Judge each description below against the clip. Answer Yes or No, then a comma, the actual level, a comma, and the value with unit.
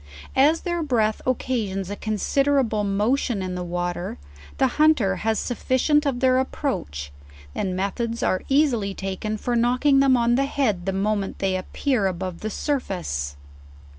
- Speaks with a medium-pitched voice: No, high, 220 Hz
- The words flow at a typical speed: Yes, average, 155 wpm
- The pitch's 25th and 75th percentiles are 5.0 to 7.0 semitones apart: Yes, wide, 5.6 semitones